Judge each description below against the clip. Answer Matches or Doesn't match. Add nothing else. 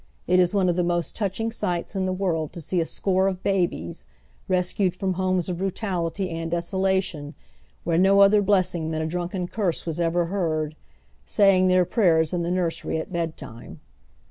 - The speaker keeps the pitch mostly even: Matches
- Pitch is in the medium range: Matches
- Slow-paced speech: Doesn't match